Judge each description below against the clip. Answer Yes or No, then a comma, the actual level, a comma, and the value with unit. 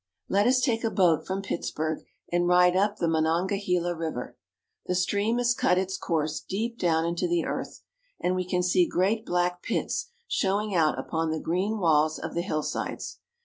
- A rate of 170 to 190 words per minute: Yes, average, 180 wpm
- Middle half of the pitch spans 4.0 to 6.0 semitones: No, average, 3.2 semitones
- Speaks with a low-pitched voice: No, medium, 180 Hz